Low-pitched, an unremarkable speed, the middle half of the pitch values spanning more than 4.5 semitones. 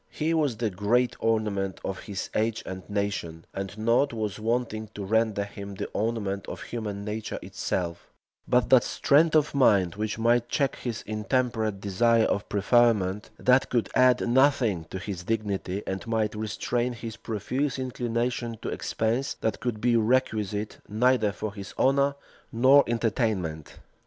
No: low, 110 Hz; average, 150 wpm; average, 3.2 semitones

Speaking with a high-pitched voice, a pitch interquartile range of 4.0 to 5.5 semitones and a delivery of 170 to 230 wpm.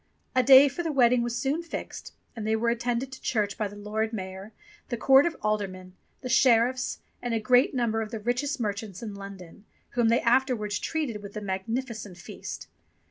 No: high, 230 Hz; average, 3.5 semitones; average, 190 wpm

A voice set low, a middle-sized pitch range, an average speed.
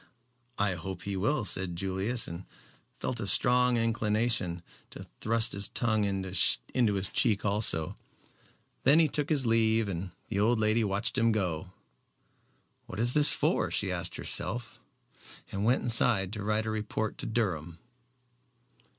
Yes: low, 110 Hz; average, 3.3 semitones; average, 150 wpm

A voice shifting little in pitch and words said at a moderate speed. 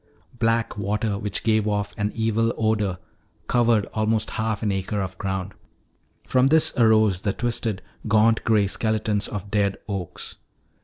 Yes: narrow, 1.8 semitones; average, 145 wpm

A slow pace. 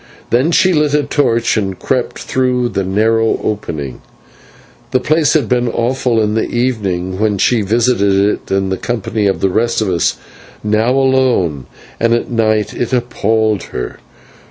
No: average, 160 wpm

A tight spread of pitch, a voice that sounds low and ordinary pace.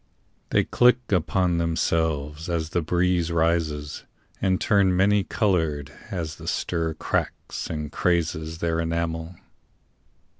No: narrow, 2.1 semitones; very low, 85 Hz; slow, 115 wpm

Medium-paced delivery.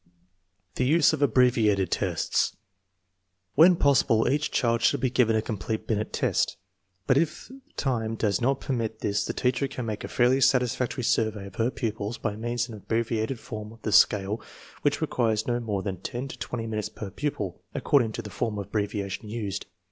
Yes: average, 185 wpm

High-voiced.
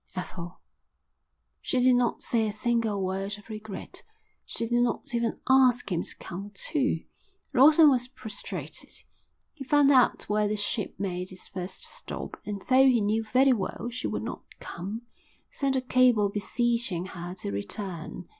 Yes: high, 220 Hz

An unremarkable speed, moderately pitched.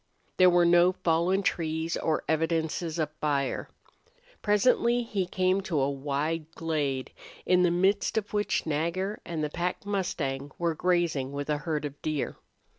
Yes: average, 155 wpm; medium, 165 Hz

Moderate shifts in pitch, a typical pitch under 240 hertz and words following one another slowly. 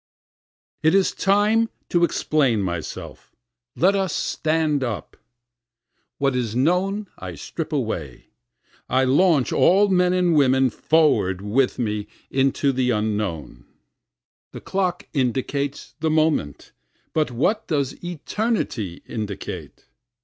No: wide, 7.3 semitones; medium, 140 Hz; slow, 115 wpm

